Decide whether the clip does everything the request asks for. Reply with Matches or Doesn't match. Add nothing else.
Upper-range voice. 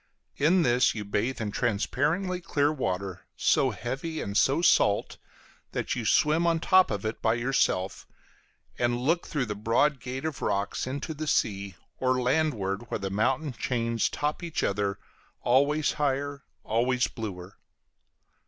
Doesn't match